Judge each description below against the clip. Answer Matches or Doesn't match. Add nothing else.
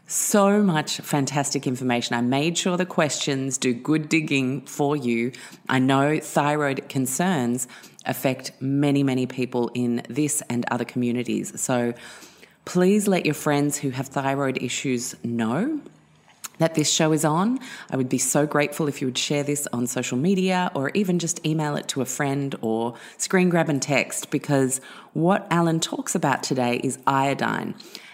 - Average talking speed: Matches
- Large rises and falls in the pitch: Doesn't match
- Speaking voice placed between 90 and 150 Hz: Matches